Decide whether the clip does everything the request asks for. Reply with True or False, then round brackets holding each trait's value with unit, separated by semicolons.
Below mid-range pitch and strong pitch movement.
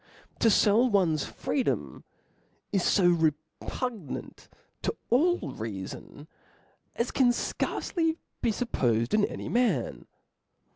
False (210 Hz; 8.0 semitones)